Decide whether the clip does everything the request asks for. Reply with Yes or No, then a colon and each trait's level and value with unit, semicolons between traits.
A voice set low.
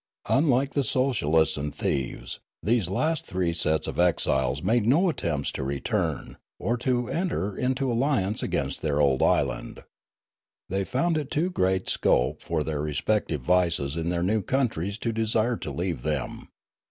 Yes: very low, 95 Hz